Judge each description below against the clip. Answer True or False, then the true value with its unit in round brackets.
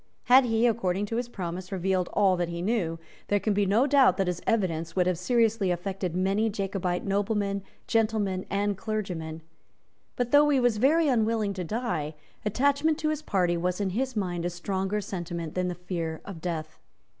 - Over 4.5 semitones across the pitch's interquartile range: False (4.1 semitones)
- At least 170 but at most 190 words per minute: True (185 wpm)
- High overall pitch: True (195 Hz)